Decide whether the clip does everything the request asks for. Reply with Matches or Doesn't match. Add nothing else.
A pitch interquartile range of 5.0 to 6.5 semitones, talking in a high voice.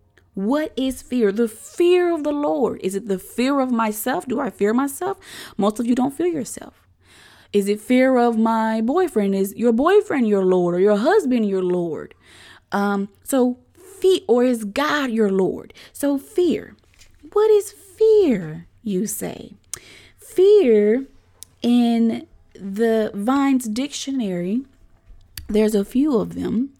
Matches